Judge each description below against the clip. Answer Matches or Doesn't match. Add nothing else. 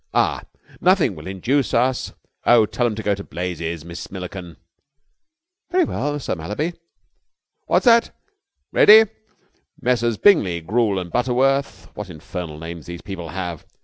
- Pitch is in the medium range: Doesn't match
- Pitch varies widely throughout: Matches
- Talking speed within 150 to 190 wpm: Doesn't match